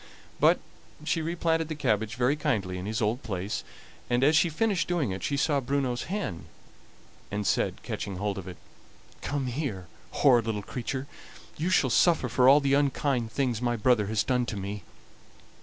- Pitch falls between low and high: No, low, 125 Hz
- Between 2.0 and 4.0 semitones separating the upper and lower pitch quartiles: No, wide, 5.6 semitones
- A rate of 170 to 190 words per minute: Yes, average, 175 wpm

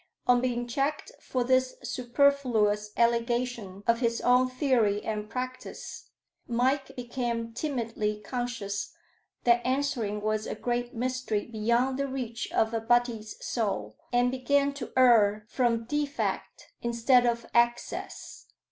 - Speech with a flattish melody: Yes, narrow, 2.3 semitones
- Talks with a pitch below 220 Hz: No, high, 240 Hz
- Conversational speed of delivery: No, slow, 125 wpm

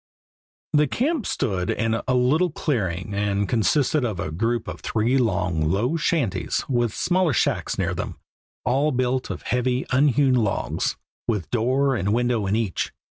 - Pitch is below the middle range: Yes, low, 120 Hz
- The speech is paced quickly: No, average, 155 wpm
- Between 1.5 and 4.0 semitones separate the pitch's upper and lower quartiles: No, average, 4.6 semitones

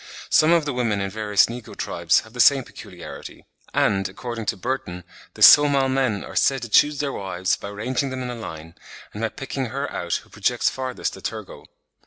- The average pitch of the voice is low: Yes, low, 120 Hz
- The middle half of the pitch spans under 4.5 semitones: No, average, 4.9 semitones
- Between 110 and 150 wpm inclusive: No, fast, 205 wpm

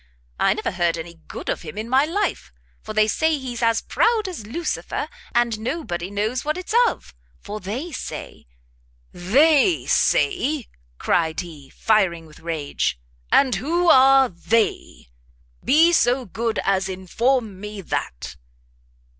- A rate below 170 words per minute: Yes, average, 145 wpm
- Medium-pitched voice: No, high, 220 Hz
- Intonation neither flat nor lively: No, wide, 7.6 semitones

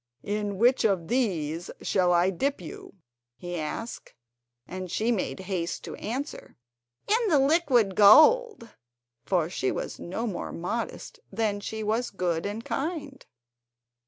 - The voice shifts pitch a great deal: Yes, wide, 6.0 semitones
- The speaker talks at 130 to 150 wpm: Yes, slow, 135 wpm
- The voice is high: Yes, high, 210 Hz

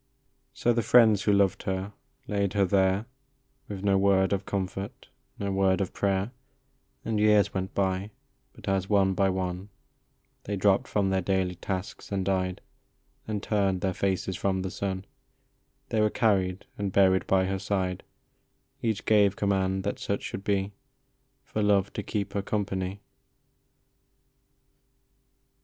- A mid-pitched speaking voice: No, very low, 95 Hz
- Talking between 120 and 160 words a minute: Yes, average, 150 wpm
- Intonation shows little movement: Yes, narrow, 1.3 semitones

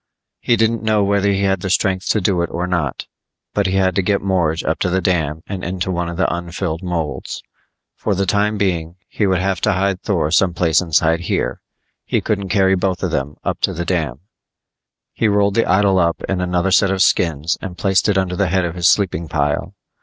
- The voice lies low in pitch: Yes, very low, 95 Hz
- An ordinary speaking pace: No, fast, 220 wpm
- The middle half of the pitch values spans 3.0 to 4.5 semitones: No, narrow, 2.4 semitones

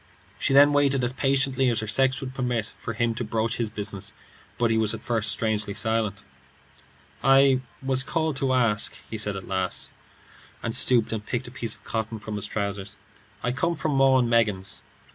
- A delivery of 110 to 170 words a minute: No, average, 195 wpm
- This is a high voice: No, low, 115 Hz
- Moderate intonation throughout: Yes, average, 3.6 semitones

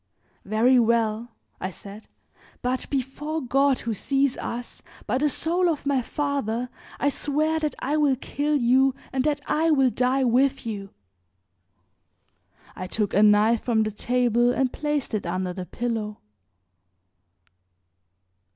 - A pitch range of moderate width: Yes, average, 4.2 semitones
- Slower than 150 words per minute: Yes, average, 140 wpm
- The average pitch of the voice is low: No, very high, 250 Hz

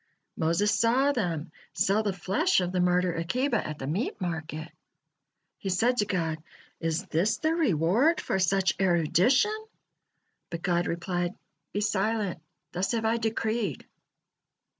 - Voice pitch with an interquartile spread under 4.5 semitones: No, average, 4.8 semitones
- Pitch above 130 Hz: Yes, high, 190 Hz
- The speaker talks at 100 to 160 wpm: Yes, average, 140 wpm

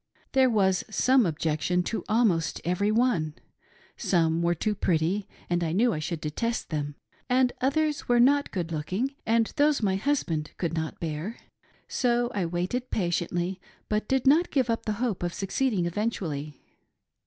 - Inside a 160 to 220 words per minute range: Yes, average, 165 wpm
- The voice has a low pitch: No, high, 195 Hz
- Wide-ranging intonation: Yes, wide, 6.4 semitones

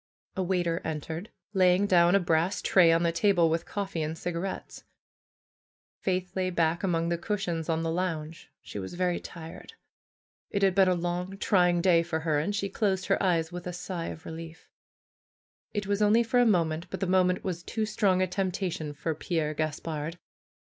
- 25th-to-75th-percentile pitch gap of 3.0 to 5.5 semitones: No, narrow, 2.5 semitones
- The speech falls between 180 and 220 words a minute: Yes, average, 185 wpm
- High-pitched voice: No, medium, 175 Hz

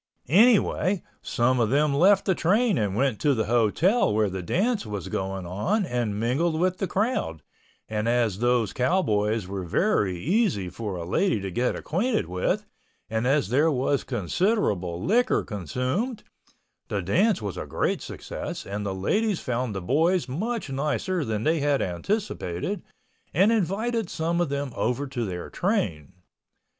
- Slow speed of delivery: No, average, 160 wpm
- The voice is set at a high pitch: No, low, 130 Hz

